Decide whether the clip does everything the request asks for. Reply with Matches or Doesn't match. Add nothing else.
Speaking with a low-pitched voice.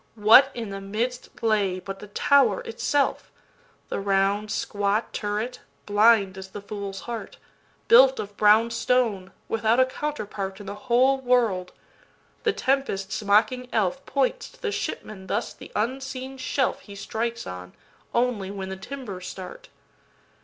Doesn't match